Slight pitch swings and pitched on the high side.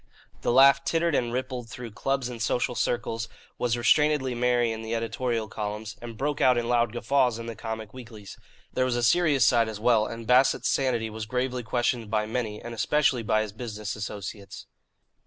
No: narrow, 2.3 semitones; low, 120 Hz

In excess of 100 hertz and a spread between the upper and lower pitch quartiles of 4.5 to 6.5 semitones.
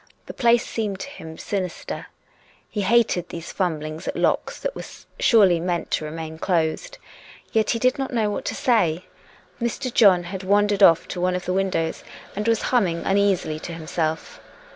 Yes: high, 190 Hz; average, 5.0 semitones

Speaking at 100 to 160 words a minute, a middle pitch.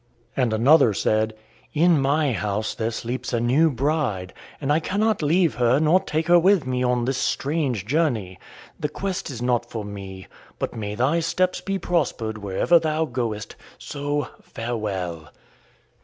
No: average, 155 wpm; low, 130 Hz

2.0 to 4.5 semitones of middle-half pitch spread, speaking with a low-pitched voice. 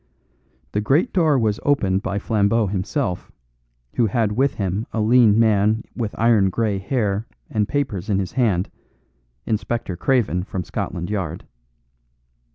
Yes: average, 3.2 semitones; low, 105 Hz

